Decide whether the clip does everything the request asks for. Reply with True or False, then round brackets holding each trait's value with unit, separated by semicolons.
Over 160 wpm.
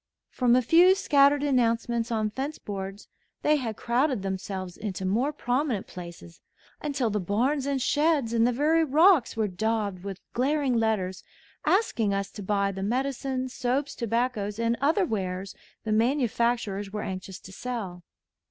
False (150 wpm)